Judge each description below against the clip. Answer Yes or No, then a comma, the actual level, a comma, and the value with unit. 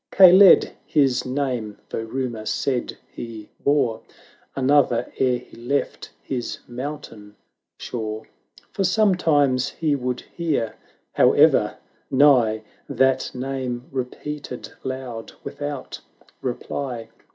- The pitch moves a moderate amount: Yes, average, 3.2 semitones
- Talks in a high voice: No, low, 130 Hz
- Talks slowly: Yes, slow, 95 wpm